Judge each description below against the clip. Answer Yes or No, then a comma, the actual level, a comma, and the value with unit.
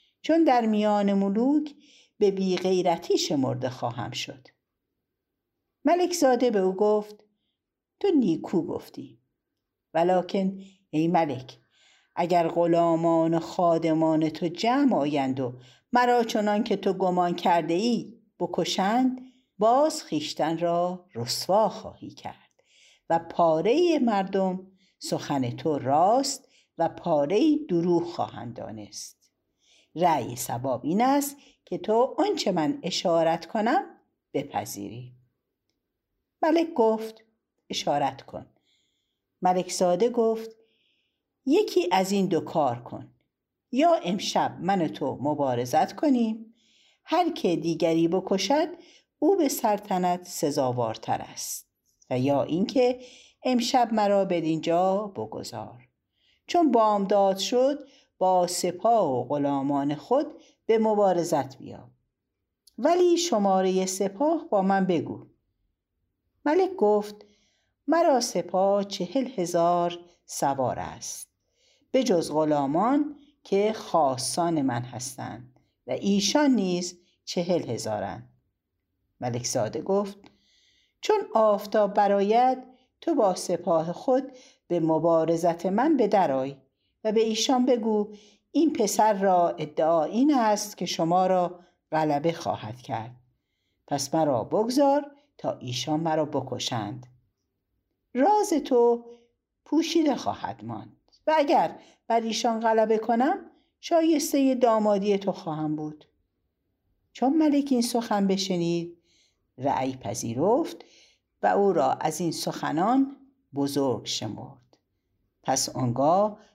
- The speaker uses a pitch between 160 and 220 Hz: Yes, high, 190 Hz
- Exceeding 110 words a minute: No, slow, 105 wpm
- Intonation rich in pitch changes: Yes, wide, 7.8 semitones